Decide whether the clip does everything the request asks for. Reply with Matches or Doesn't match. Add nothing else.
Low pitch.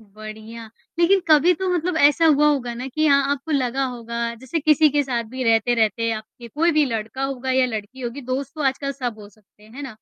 Doesn't match